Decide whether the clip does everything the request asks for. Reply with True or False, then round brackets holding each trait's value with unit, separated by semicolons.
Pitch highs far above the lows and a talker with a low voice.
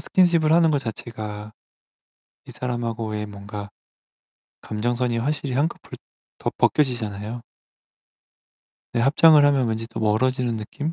False (4.8 semitones; 120 Hz)